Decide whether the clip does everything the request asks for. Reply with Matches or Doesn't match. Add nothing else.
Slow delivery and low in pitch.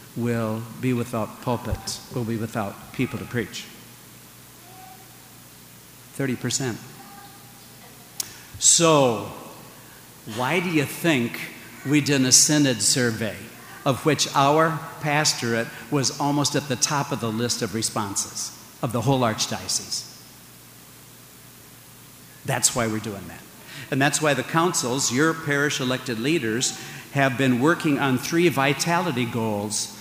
Matches